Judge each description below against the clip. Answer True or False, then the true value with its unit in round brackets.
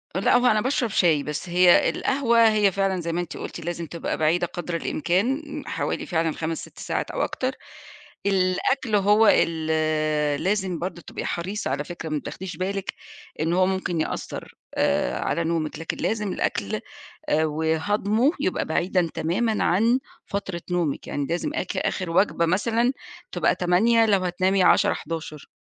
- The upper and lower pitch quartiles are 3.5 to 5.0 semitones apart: True (4.1 semitones)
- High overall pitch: False (180 Hz)